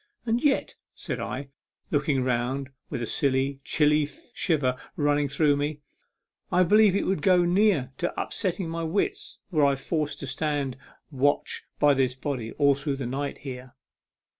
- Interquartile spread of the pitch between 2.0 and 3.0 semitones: No, average, 3.4 semitones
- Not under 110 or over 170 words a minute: Yes, average, 165 wpm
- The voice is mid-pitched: Yes, medium, 145 Hz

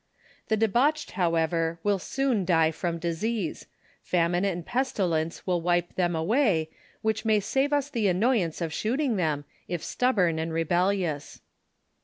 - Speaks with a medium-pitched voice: Yes, medium, 180 Hz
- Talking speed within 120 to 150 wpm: Yes, average, 140 wpm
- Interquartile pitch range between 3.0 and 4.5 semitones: No, average, 5.1 semitones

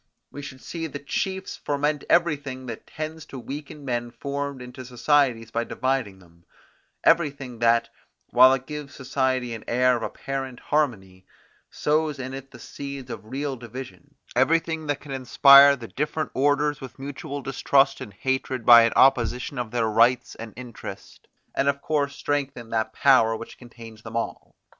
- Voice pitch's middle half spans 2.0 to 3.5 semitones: Yes, average, 3.2 semitones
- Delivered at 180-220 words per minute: No, average, 160 wpm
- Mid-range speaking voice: No, low, 130 Hz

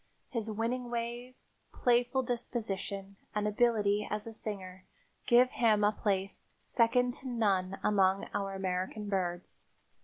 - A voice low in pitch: No, high, 210 Hz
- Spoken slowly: Yes, slow, 125 wpm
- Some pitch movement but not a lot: Yes, average, 3.5 semitones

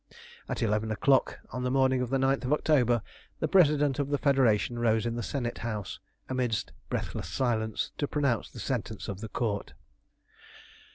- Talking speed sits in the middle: Yes, average, 170 wpm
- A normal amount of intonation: Yes, average, 3.4 semitones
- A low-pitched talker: Yes, low, 125 Hz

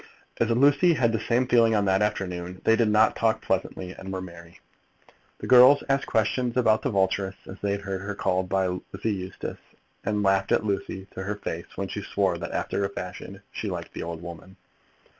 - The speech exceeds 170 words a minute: Yes, average, 200 wpm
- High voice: No, low, 100 Hz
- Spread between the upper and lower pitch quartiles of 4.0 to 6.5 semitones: No, average, 3.1 semitones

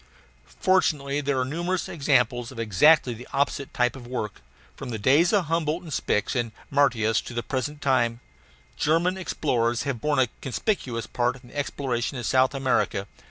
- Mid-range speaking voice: No, low, 130 Hz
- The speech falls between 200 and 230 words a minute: No, average, 170 wpm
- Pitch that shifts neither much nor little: Yes, average, 3.7 semitones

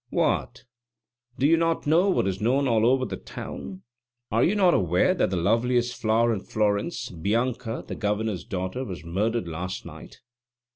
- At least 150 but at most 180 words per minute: Yes, average, 165 wpm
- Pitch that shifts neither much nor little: Yes, average, 4.9 semitones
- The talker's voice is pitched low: Yes, low, 115 Hz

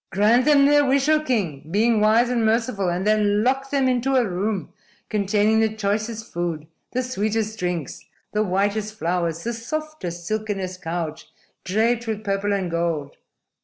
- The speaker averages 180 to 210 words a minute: No, average, 160 wpm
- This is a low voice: No, high, 215 Hz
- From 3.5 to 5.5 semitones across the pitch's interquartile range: Yes, average, 4.3 semitones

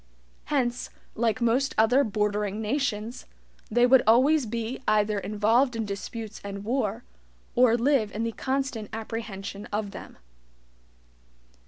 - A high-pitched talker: Yes, high, 225 Hz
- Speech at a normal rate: No, slow, 125 wpm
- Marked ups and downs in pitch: No, average, 2.9 semitones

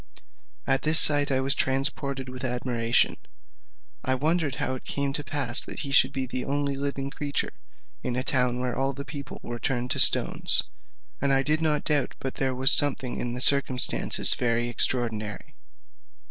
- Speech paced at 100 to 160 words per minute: No, average, 175 wpm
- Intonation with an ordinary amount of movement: No, narrow, 2.0 semitones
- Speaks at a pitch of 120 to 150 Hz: Yes, low, 135 Hz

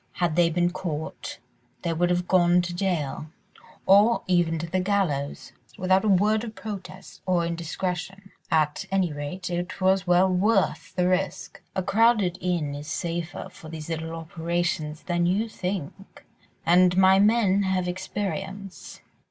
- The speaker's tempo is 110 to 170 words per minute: Yes, average, 150 wpm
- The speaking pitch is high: No, medium, 180 Hz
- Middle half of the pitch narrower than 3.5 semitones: Yes, narrow, 2.4 semitones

